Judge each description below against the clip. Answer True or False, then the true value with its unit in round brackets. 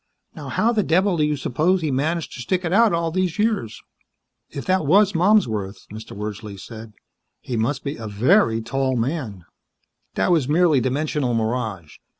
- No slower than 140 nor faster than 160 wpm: False (170 wpm)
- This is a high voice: False (140 Hz)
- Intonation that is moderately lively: False (7.6 semitones)